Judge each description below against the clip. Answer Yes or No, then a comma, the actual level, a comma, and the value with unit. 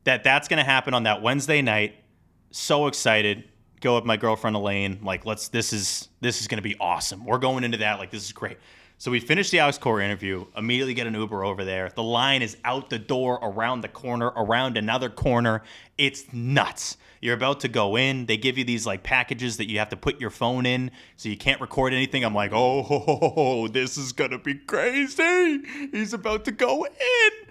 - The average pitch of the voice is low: Yes, low, 120 Hz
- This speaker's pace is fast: Yes, fast, 210 wpm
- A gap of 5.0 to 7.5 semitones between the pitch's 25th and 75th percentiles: No, average, 4.0 semitones